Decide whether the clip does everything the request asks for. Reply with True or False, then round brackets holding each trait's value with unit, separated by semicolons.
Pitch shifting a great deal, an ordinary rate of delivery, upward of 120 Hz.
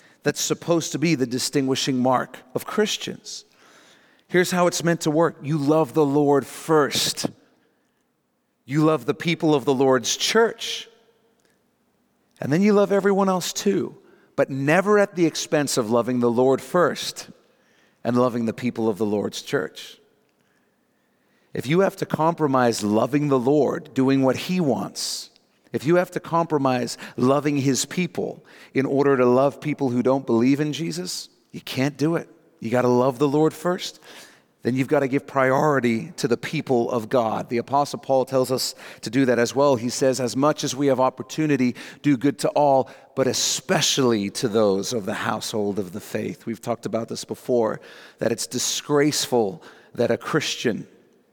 False (4.2 semitones; 175 wpm; 140 Hz)